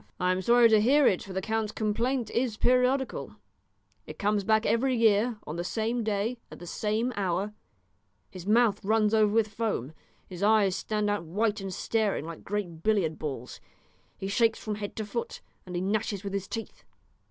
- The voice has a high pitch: Yes, high, 210 Hz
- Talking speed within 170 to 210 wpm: Yes, average, 185 wpm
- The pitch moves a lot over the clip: No, average, 2.7 semitones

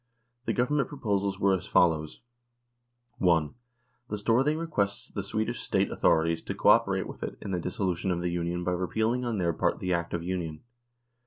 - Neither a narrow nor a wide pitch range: Yes, average, 4.2 semitones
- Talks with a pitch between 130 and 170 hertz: No, very low, 95 Hz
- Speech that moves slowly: No, average, 180 wpm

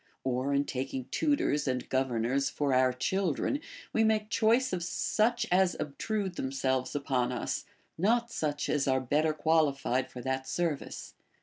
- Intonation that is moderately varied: No, wide, 6.4 semitones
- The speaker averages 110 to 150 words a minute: Yes, average, 145 wpm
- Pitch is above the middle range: No, medium, 145 Hz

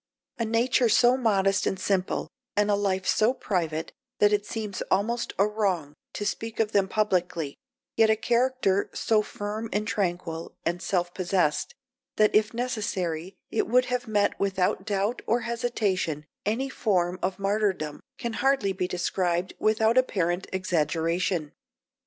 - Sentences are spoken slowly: No, average, 145 wpm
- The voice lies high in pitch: Yes, high, 200 Hz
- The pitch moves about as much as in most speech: Yes, average, 3.5 semitones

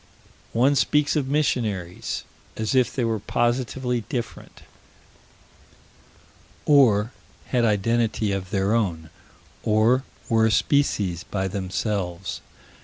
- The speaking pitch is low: Yes, low, 110 Hz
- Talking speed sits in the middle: No, slow, 105 wpm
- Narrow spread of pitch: No, average, 4.3 semitones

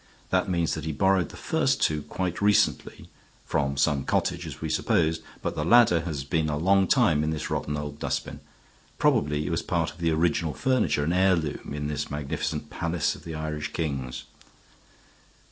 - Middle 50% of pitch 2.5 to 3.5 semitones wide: Yes, average, 2.9 semitones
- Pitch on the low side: Yes, very low, 80 Hz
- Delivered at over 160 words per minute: Yes, average, 180 wpm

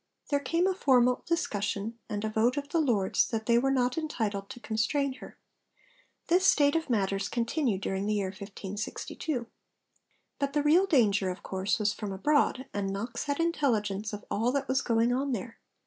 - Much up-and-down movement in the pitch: Yes, wide, 5.7 semitones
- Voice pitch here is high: Yes, high, 235 Hz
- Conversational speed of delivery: Yes, average, 180 wpm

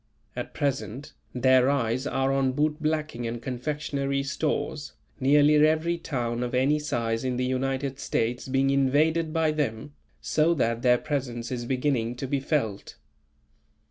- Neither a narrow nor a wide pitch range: Yes, average, 3.1 semitones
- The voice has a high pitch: No, low, 135 Hz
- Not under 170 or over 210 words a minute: No, average, 140 wpm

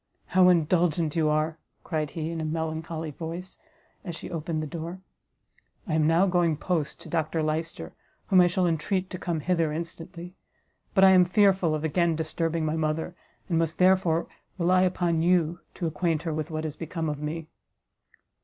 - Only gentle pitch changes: Yes, narrow, 2.1 semitones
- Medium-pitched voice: Yes, medium, 165 Hz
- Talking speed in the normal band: Yes, average, 175 wpm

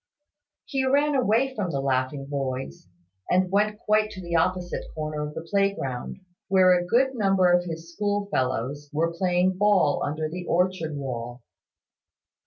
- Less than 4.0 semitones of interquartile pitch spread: No, wide, 5.5 semitones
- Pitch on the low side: No, medium, 175 Hz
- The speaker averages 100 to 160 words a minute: Yes, average, 150 wpm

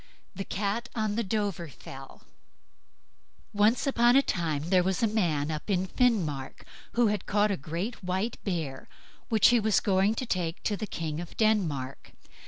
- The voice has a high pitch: Yes, high, 195 Hz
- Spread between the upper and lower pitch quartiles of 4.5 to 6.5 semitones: Yes, average, 4.8 semitones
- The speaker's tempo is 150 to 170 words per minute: Yes, average, 165 wpm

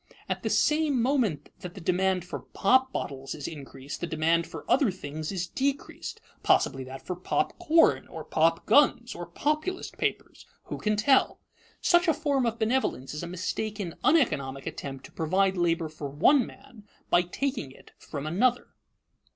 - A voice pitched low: No, medium, 185 Hz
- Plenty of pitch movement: Yes, wide, 8.7 semitones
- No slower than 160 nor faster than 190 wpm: Yes, average, 165 wpm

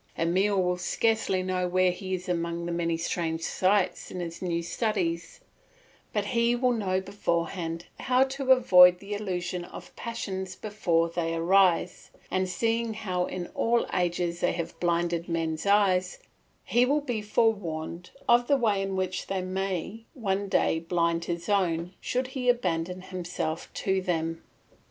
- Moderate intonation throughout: Yes, average, 3.4 semitones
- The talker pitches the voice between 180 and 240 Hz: Yes, medium, 185 Hz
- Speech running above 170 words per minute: No, average, 155 wpm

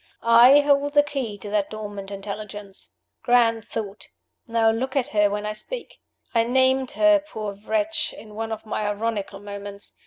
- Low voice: No, high, 225 Hz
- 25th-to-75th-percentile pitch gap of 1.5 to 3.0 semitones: No, average, 4.2 semitones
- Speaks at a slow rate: No, average, 165 wpm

